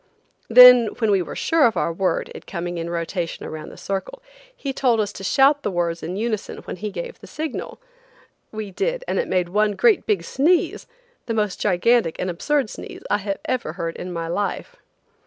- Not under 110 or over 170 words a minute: No, average, 195 wpm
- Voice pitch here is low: No, high, 210 Hz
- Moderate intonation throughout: No, wide, 7.4 semitones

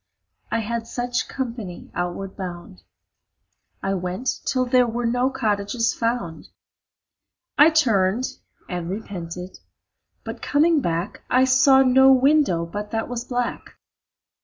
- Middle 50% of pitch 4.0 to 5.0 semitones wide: No, wide, 5.4 semitones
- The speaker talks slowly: Yes, slow, 120 wpm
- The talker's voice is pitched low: No, high, 230 Hz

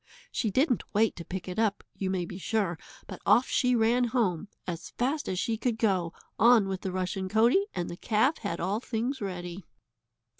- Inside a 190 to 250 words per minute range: Yes, average, 195 wpm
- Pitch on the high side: Yes, high, 210 Hz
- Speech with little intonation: No, average, 4.3 semitones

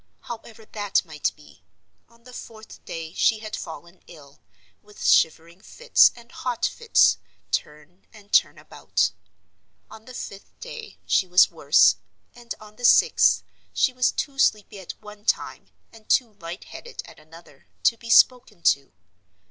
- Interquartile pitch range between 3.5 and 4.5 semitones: No, wide, 5.5 semitones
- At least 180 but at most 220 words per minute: No, average, 155 wpm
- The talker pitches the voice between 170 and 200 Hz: No, high, 210 Hz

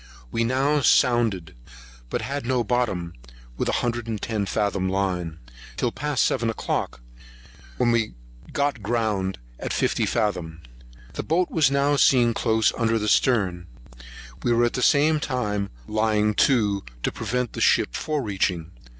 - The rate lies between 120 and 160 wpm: Yes, average, 150 wpm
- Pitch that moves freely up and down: No, average, 4.1 semitones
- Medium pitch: No, low, 115 Hz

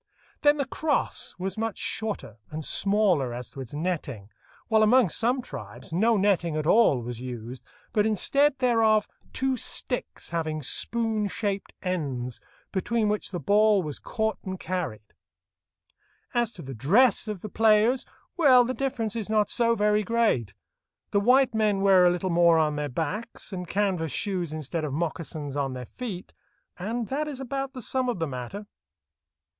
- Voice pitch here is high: Yes, high, 200 Hz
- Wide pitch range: Yes, wide, 6.5 semitones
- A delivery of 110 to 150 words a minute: No, average, 165 wpm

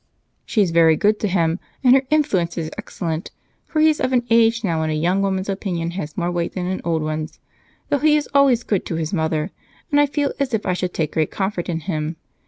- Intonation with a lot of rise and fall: Yes, wide, 6.0 semitones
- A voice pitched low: No, medium, 185 Hz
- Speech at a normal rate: No, fast, 235 wpm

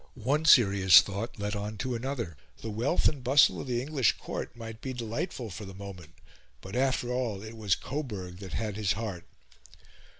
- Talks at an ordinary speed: Yes, average, 190 wpm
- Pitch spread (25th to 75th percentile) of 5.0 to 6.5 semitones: No, average, 4.2 semitones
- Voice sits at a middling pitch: No, low, 110 Hz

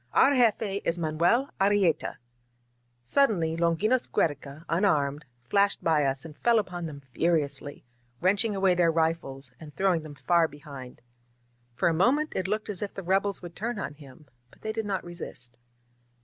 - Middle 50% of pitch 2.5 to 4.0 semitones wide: No, average, 5.3 semitones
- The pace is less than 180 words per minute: Yes, average, 165 wpm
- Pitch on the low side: No, medium, 170 Hz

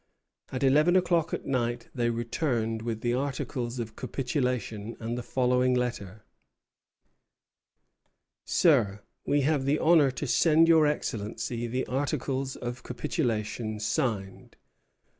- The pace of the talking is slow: Yes, slow, 120 wpm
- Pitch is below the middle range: Yes, low, 125 Hz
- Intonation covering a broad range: No, average, 3.6 semitones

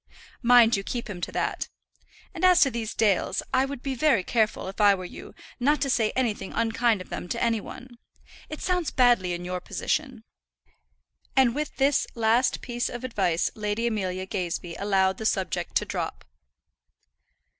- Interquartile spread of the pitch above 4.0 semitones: Yes, average, 4.7 semitones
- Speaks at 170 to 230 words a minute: Yes, average, 175 wpm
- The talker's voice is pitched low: No, high, 230 Hz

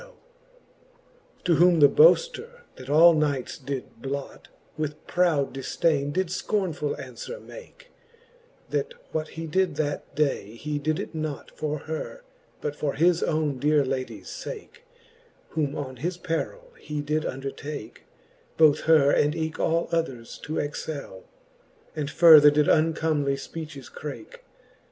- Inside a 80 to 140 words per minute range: Yes, slow, 135 wpm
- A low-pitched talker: No, medium, 155 Hz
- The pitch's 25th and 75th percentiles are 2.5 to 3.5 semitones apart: Yes, average, 2.8 semitones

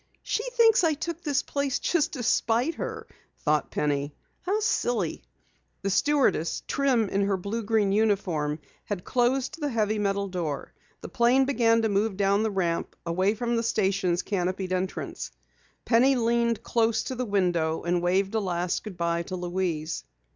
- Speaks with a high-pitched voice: Yes, high, 205 Hz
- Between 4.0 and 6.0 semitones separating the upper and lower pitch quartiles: Yes, average, 5.0 semitones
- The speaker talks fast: No, average, 165 wpm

